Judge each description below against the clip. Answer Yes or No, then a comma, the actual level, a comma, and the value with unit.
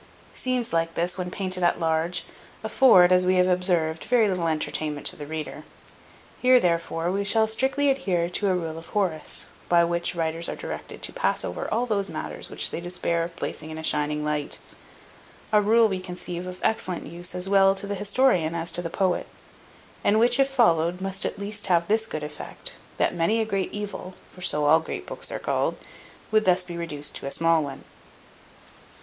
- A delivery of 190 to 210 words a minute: Yes, average, 200 wpm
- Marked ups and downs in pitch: No, average, 3.5 semitones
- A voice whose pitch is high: No, medium, 180 Hz